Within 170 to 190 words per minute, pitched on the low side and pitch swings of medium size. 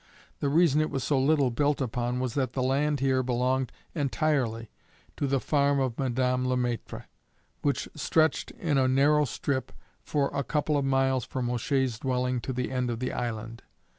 No: average, 180 wpm; low, 130 Hz; narrow, 2.1 semitones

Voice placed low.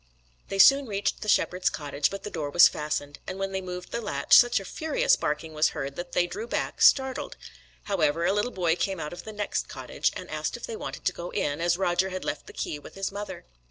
No: medium, 185 Hz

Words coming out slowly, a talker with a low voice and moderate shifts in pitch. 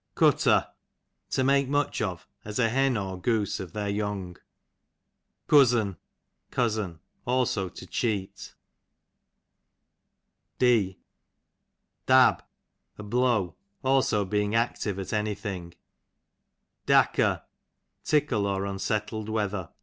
Yes: slow, 105 wpm; low, 105 Hz; average, 3.7 semitones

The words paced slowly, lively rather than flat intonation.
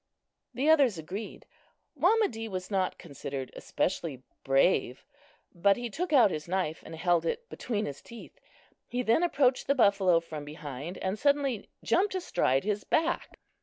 No: average, 150 wpm; wide, 7.8 semitones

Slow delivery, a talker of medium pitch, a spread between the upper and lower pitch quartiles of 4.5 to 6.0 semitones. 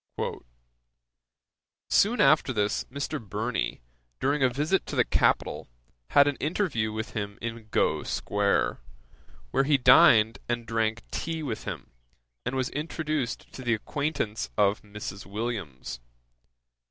No: slow, 130 wpm; low, 120 Hz; average, 5.1 semitones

